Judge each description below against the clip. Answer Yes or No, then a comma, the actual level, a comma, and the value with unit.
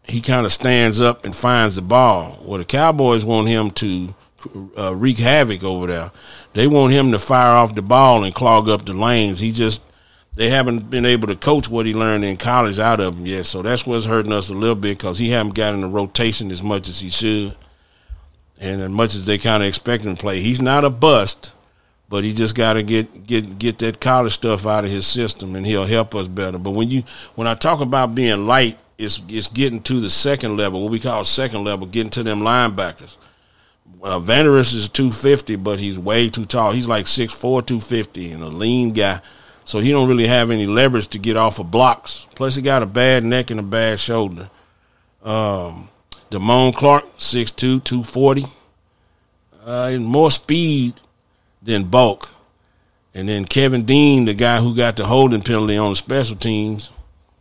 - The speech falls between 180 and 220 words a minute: Yes, average, 200 wpm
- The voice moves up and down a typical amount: Yes, average, 3.7 semitones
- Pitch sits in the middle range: No, low, 110 Hz